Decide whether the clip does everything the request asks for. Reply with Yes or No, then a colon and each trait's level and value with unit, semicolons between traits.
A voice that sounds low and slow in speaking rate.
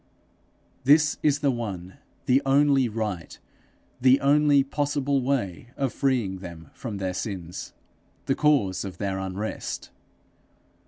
Yes: low, 125 Hz; slow, 120 wpm